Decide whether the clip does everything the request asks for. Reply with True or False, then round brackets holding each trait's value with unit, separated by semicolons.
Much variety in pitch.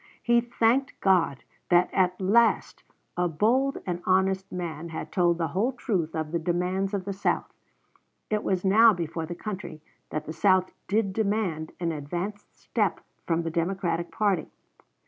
False (3.4 semitones)